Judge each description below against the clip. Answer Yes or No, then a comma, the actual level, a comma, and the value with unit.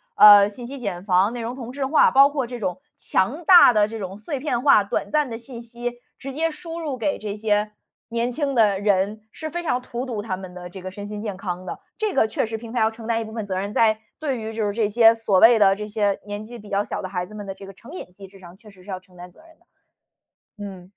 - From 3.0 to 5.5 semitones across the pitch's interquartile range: Yes, average, 3.7 semitones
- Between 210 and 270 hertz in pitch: Yes, high, 220 Hz